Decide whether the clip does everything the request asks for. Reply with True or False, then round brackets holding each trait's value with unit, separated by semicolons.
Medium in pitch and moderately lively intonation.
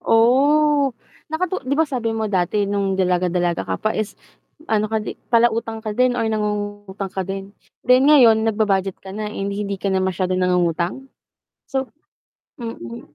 False (215 Hz; 3.8 semitones)